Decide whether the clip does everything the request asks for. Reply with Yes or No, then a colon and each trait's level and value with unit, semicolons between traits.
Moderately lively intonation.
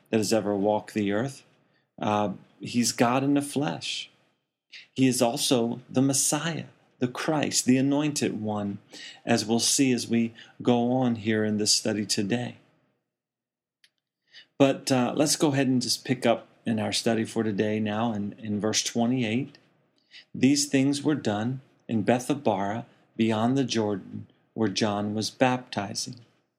Yes: average, 3.7 semitones